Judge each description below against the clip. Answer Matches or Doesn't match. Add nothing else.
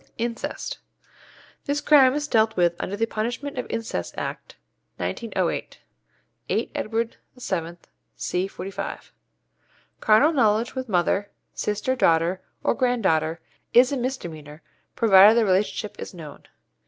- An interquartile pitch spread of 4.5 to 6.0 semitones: Matches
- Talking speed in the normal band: Doesn't match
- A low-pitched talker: Doesn't match